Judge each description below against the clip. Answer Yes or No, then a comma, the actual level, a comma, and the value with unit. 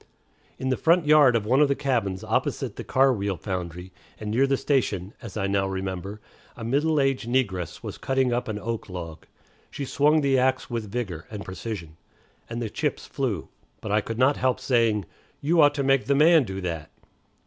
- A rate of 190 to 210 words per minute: Yes, average, 200 wpm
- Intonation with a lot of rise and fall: Yes, wide, 5.7 semitones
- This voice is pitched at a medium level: No, low, 115 Hz